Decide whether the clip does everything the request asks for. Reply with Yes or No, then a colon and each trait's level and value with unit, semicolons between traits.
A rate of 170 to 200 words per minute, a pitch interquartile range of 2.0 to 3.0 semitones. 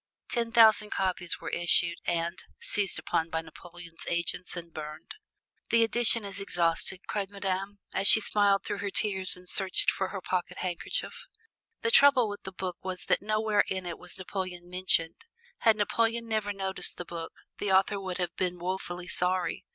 Yes: average, 175 wpm; average, 2.7 semitones